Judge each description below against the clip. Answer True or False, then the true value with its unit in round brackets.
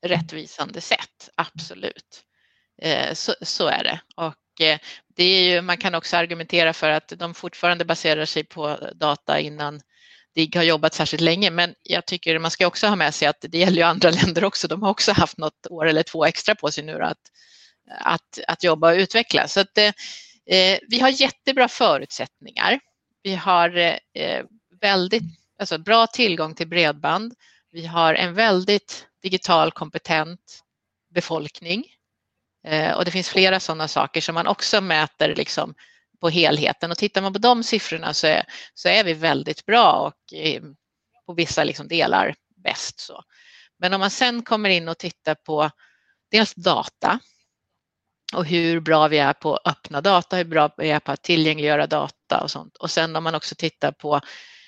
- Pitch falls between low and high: True (170 Hz)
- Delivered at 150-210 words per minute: True (170 wpm)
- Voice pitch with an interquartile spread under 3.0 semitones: False (3.3 semitones)